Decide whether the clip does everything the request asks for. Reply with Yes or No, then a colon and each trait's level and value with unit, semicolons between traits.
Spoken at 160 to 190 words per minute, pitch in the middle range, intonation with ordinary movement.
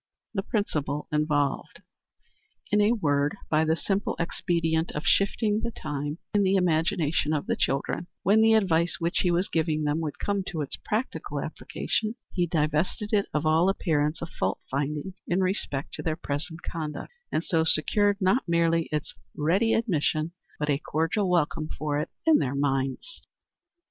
Yes: average, 165 wpm; medium, 165 Hz; average, 4.4 semitones